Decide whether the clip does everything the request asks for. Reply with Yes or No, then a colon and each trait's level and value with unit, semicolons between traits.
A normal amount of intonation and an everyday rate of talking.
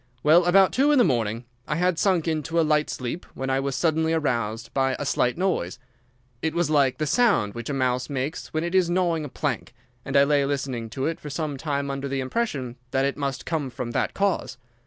No: average, 4.1 semitones; fast, 225 wpm